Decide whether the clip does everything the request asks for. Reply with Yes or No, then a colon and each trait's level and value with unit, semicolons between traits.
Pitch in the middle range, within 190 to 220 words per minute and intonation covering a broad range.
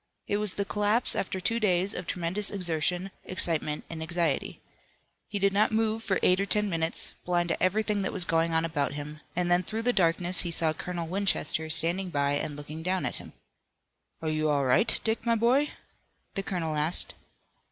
No: medium, 180 Hz; average, 195 wpm; average, 3.8 semitones